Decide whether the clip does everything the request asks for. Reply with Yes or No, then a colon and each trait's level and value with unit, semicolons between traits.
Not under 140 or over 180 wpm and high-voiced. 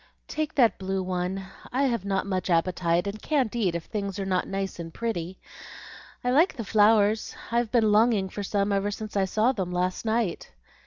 No: average, 195 wpm; high, 200 Hz